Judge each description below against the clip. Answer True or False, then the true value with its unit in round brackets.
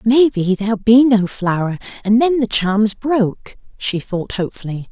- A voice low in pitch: False (215 Hz)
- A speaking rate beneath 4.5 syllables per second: False (4.6 syllables/s)